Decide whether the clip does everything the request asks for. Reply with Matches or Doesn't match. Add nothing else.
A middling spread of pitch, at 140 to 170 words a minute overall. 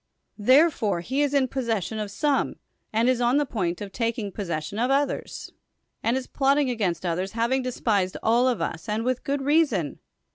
Doesn't match